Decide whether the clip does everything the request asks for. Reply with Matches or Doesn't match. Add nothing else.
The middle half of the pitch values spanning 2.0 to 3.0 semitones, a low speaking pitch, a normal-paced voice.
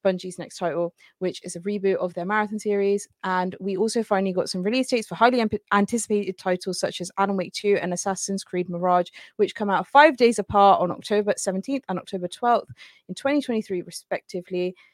Doesn't match